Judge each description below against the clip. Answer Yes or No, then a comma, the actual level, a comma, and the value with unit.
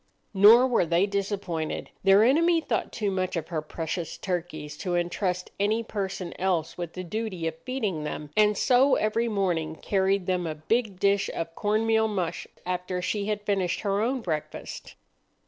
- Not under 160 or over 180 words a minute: Yes, average, 170 wpm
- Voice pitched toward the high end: Yes, high, 195 Hz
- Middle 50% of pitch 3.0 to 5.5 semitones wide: Yes, average, 3.6 semitones